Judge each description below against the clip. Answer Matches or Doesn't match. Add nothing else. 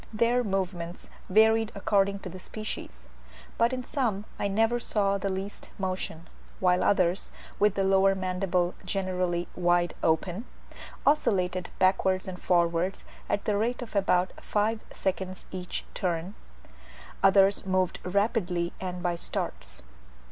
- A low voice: Doesn't match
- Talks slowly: Matches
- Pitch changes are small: Matches